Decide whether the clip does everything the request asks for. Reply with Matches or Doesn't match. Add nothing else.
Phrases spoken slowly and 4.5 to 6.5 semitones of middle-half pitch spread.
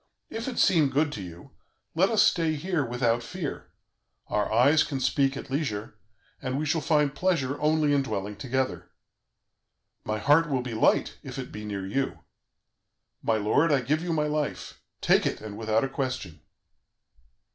Doesn't match